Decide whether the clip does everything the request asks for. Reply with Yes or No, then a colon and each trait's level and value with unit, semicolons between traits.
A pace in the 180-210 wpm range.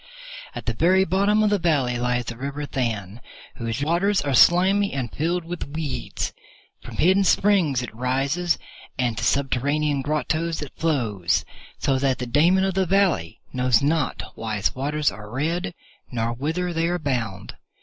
No: average, 165 wpm